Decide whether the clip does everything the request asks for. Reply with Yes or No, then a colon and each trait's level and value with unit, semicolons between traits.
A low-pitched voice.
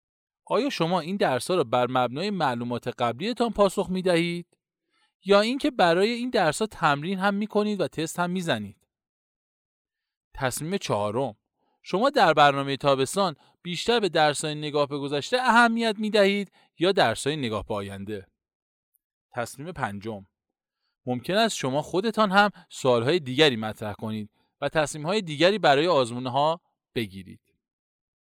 No: medium, 155 Hz